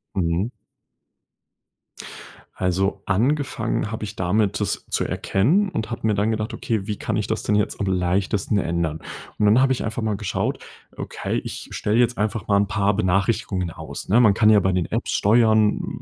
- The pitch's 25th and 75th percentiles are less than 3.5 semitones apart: Yes, narrow, 2.6 semitones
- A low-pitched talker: Yes, low, 105 Hz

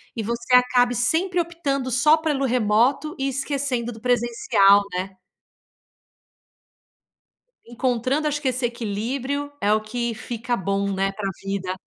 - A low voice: No, high, 245 Hz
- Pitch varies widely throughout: No, average, 4.3 semitones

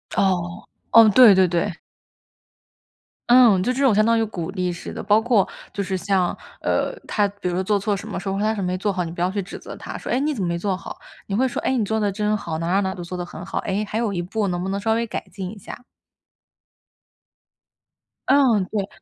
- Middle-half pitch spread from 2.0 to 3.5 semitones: Yes, average, 3.1 semitones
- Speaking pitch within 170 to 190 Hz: No, high, 200 Hz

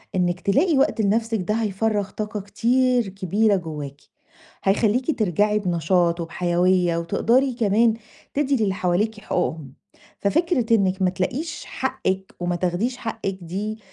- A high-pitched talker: Yes, high, 200 Hz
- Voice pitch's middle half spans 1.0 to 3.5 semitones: No, average, 4.0 semitones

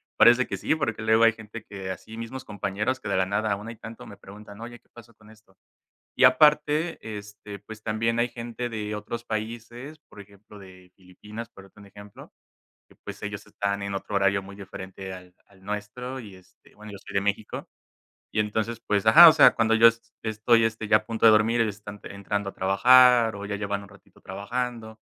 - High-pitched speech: No, low, 105 Hz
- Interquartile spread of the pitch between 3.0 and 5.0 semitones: No, narrow, 2.5 semitones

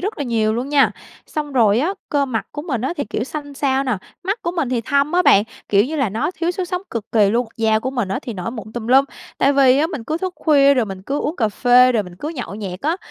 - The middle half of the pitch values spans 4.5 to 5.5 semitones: Yes, average, 4.9 semitones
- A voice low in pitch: No, very high, 260 Hz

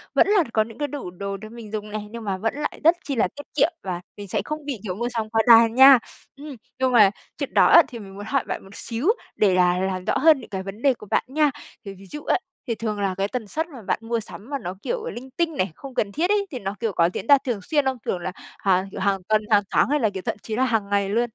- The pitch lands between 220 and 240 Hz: Yes, high, 225 Hz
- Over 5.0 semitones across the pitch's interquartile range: Yes, wide, 5.4 semitones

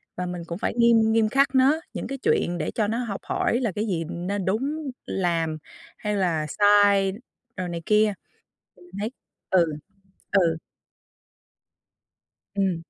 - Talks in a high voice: Yes, high, 205 Hz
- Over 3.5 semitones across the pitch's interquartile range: Yes, average, 4.3 semitones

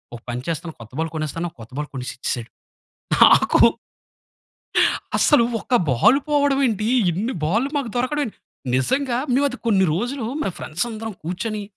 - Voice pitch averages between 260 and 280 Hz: No, high, 215 Hz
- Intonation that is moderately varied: No, wide, 8.0 semitones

